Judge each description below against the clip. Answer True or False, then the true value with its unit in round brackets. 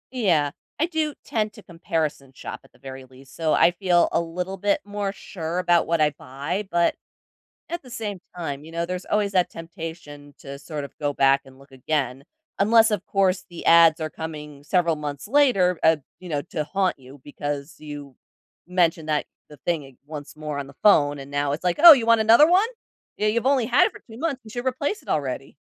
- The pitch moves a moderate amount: False (6.0 semitones)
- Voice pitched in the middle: True (170 Hz)